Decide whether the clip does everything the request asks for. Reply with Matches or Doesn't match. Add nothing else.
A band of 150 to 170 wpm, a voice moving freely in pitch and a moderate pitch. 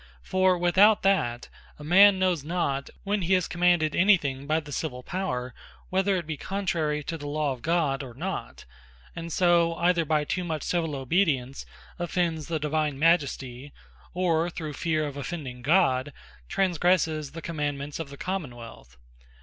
Doesn't match